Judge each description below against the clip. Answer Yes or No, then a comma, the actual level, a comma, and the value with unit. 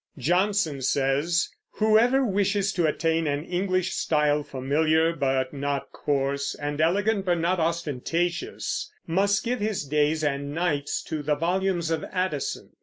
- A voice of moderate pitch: Yes, medium, 165 Hz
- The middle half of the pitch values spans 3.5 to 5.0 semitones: Yes, average, 4.5 semitones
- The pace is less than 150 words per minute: Yes, slow, 135 wpm